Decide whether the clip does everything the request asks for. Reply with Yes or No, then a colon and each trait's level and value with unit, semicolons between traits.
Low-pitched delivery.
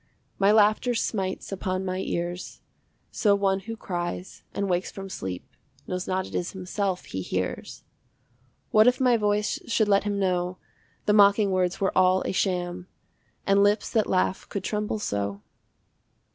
No: high, 190 Hz